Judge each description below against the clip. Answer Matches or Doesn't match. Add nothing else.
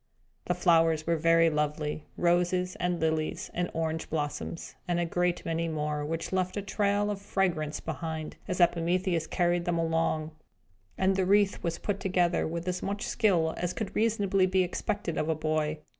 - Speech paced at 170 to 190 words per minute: Matches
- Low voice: Doesn't match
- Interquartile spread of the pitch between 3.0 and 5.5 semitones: Doesn't match